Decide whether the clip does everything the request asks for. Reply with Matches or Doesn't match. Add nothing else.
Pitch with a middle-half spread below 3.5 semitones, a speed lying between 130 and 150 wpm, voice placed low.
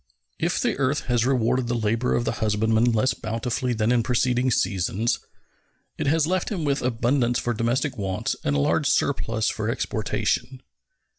Doesn't match